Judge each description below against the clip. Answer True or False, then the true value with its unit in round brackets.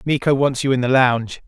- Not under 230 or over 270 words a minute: True (245 wpm)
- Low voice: True (130 Hz)